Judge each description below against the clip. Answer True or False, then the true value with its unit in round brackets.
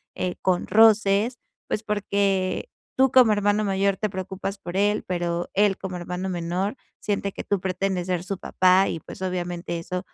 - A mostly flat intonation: True (2.2 semitones)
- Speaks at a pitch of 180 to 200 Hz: True (190 Hz)